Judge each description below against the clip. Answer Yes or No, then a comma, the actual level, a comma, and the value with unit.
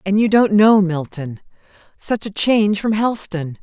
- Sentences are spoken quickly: No, average, 165 wpm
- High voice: Yes, high, 195 Hz